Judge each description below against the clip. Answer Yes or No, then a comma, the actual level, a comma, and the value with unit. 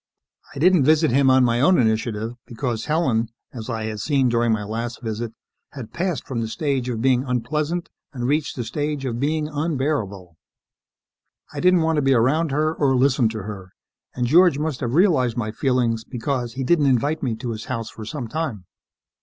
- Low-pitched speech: Yes, low, 130 Hz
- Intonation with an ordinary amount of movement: Yes, average, 4.6 semitones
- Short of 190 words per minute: No, average, 195 wpm